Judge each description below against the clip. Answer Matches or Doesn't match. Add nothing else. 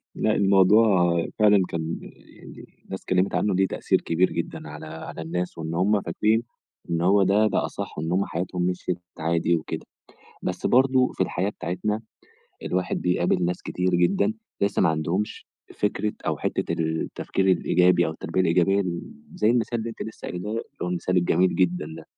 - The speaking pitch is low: Matches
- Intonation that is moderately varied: Matches